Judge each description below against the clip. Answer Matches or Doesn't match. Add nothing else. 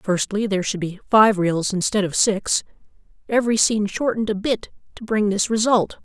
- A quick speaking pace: Doesn't match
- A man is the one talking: Doesn't match